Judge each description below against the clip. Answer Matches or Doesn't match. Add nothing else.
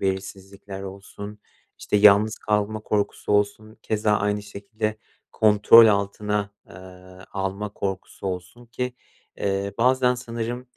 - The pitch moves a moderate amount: Doesn't match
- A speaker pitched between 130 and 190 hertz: Doesn't match